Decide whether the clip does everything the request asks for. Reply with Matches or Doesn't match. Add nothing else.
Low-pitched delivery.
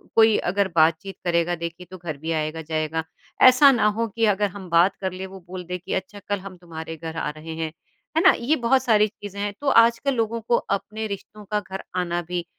Doesn't match